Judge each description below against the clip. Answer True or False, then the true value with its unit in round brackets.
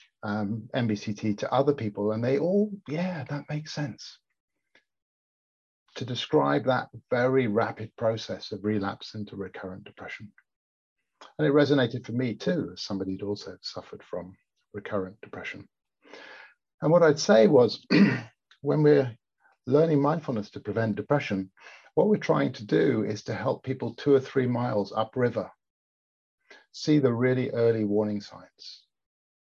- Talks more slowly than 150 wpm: True (140 wpm)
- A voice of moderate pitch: False (115 Hz)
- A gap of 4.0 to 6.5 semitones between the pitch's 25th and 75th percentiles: True (5.2 semitones)